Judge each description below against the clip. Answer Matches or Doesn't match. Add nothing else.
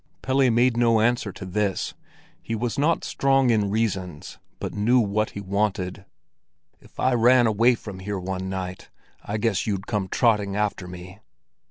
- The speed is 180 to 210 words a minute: Doesn't match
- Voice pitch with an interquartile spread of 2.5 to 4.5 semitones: Matches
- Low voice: Matches